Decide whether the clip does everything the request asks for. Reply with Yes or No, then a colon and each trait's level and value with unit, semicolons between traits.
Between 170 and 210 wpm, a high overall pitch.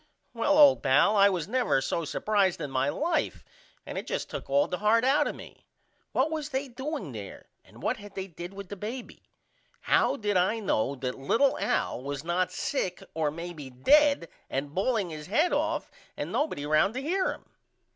Yes: average, 195 wpm; high, 200 Hz